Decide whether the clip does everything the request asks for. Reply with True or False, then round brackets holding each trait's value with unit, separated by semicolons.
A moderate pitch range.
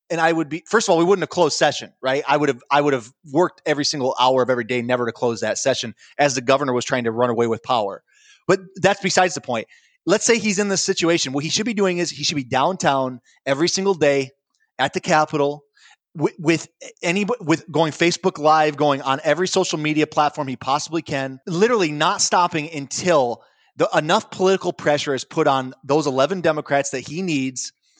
True (5.0 semitones)